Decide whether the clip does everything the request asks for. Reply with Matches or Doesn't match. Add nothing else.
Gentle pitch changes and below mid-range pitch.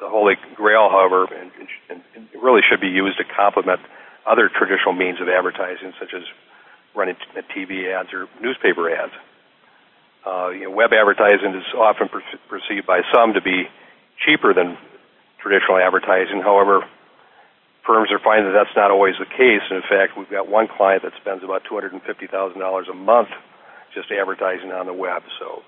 Matches